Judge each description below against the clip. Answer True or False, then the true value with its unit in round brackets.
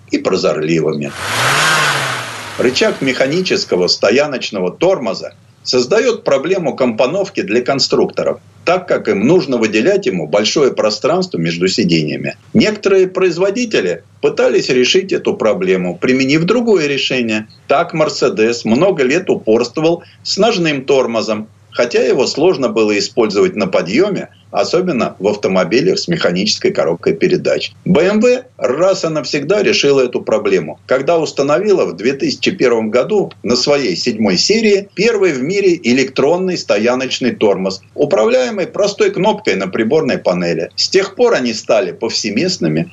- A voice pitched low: False (150 Hz)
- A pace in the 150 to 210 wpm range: False (120 wpm)